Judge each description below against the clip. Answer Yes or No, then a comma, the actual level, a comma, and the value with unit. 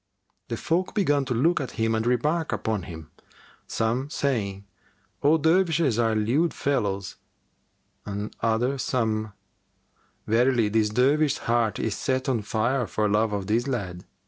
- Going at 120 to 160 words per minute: Yes, average, 145 wpm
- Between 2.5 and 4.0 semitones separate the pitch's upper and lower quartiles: No, average, 4.4 semitones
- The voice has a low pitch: Yes, low, 115 Hz